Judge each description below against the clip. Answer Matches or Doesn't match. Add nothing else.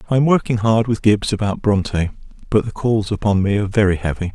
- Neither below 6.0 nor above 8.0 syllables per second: Matches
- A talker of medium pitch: Doesn't match